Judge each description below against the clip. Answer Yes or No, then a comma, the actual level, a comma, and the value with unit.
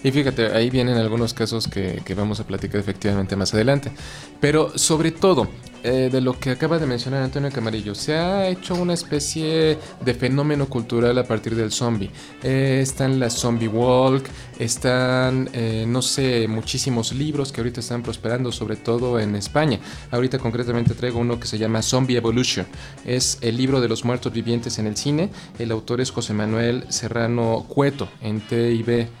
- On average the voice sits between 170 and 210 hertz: No, low, 120 Hz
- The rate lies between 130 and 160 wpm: No, average, 175 wpm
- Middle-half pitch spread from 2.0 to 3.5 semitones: Yes, average, 2.8 semitones